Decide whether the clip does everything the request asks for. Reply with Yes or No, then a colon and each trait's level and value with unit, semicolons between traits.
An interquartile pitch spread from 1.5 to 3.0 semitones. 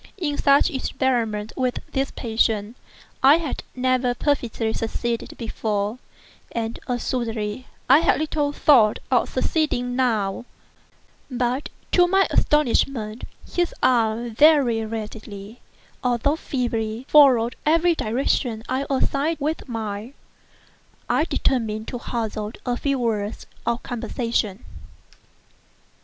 No: average, 3.7 semitones